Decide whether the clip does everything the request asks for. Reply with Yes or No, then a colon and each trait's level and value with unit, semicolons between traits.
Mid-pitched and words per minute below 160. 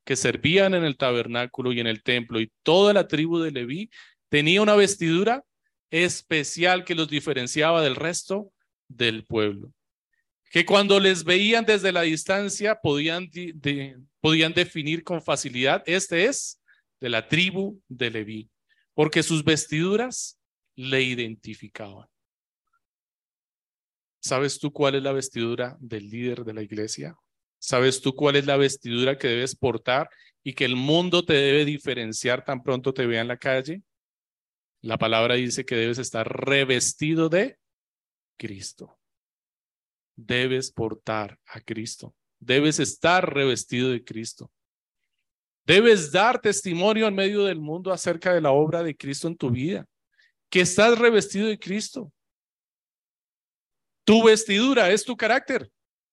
Yes: medium, 150 Hz; average, 140 wpm